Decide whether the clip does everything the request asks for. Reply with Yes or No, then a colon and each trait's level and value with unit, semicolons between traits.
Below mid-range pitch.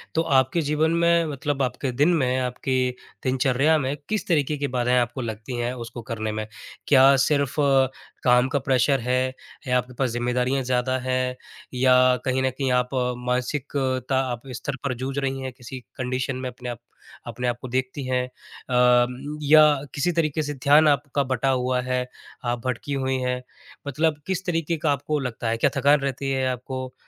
Yes: low, 130 Hz